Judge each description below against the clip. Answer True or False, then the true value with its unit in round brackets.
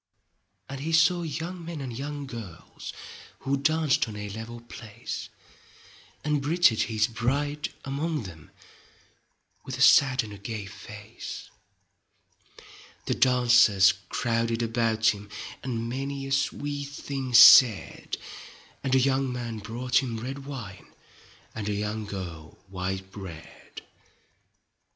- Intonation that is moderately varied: True (4.4 semitones)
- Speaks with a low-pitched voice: True (125 Hz)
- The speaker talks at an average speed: False (125 wpm)